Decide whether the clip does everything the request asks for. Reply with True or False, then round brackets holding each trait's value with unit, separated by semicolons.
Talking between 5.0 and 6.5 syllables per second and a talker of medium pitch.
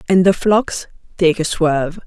False (4.4 syllables/s; 175 Hz)